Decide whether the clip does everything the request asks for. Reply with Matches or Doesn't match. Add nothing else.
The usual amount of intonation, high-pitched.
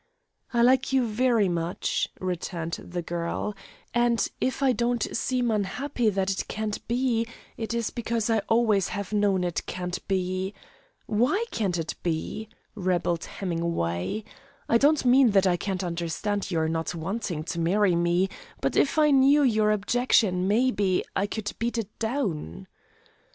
Matches